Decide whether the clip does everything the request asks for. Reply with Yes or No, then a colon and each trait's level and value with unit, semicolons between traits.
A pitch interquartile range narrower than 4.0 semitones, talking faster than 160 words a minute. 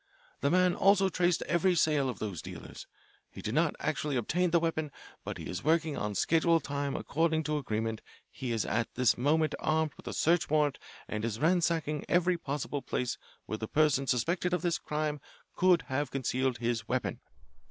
No: average, 4.7 semitones; average, 185 wpm